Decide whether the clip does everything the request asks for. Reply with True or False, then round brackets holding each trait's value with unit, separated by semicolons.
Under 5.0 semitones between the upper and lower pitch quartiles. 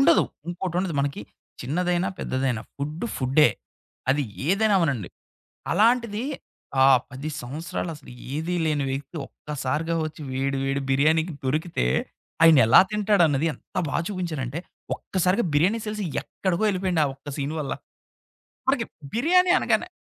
False (5.3 semitones)